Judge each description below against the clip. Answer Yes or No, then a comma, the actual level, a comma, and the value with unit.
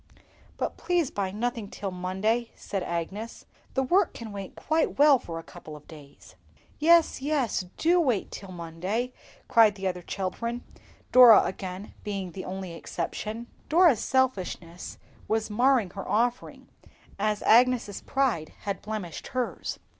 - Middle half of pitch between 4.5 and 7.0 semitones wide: Yes, average, 5.3 semitones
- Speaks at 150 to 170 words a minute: No, average, 140 wpm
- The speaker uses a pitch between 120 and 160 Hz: No, high, 215 Hz